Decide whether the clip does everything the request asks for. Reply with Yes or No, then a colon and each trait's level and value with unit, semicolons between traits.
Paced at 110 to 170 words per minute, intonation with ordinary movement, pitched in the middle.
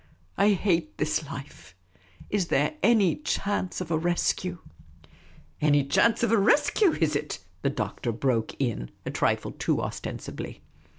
No: average, 165 wpm; wide, 6.8 semitones; medium, 160 Hz